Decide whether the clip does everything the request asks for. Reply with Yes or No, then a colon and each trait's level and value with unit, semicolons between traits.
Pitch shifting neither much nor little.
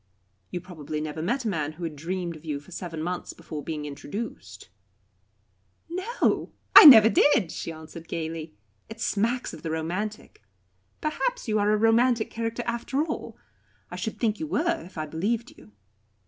No: wide, 6.6 semitones